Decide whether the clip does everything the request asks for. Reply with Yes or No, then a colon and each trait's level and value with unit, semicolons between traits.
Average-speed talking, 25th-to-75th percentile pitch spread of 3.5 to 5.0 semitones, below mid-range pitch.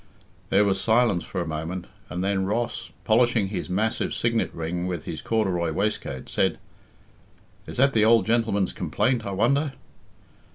Yes: average, 155 wpm; average, 4.1 semitones; low, 100 Hz